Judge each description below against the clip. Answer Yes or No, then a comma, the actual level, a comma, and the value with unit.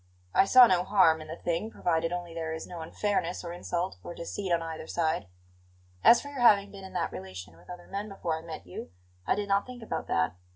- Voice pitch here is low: No, medium, 175 Hz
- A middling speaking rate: No, fast, 235 wpm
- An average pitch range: Yes, average, 3.7 semitones